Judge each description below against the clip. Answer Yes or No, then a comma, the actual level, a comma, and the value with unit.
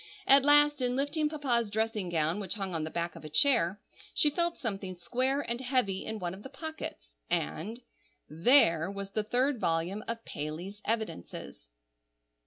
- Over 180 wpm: No, average, 165 wpm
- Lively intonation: Yes, wide, 7.2 semitones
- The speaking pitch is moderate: No, high, 215 Hz